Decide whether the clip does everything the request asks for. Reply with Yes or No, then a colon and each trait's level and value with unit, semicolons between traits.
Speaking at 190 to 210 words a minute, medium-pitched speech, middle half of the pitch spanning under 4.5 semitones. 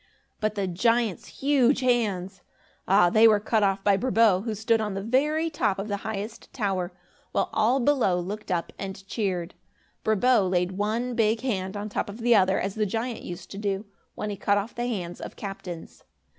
No: average, 195 wpm; high, 210 Hz; average, 3.1 semitones